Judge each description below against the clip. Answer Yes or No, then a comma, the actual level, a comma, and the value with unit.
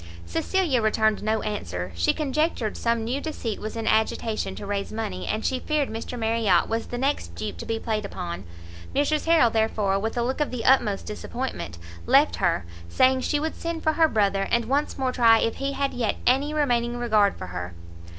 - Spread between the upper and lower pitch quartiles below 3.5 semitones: No, average, 4.4 semitones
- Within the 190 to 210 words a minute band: Yes, average, 200 wpm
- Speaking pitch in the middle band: No, high, 230 Hz